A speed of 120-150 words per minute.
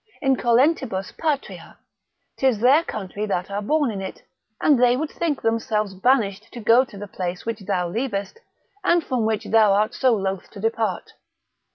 No: average, 170 wpm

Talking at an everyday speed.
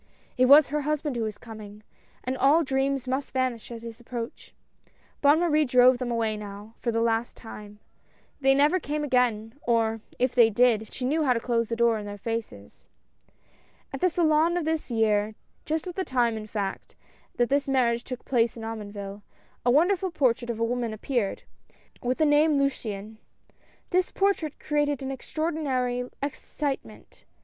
Yes: average, 180 wpm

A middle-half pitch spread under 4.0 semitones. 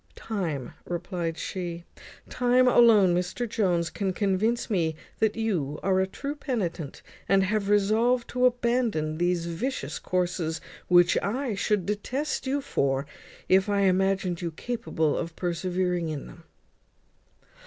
No: average, 4.6 semitones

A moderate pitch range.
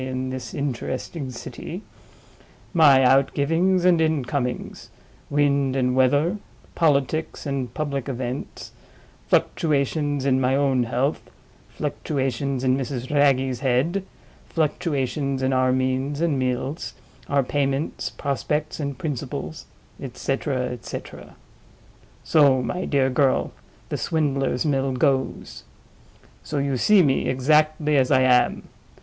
No: narrow, 2.3 semitones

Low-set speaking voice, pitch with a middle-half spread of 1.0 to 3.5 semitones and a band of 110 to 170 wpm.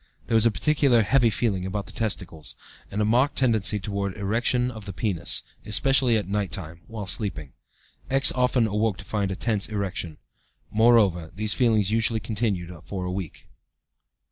Yes: low, 105 Hz; average, 3.2 semitones; average, 165 wpm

